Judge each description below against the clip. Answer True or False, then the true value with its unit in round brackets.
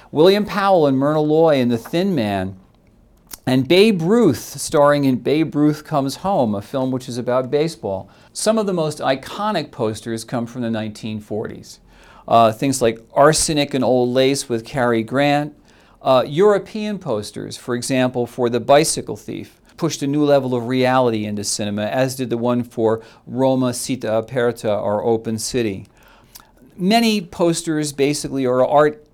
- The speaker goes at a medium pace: True (160 wpm)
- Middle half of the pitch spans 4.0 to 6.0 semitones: True (4.5 semitones)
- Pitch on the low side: True (130 Hz)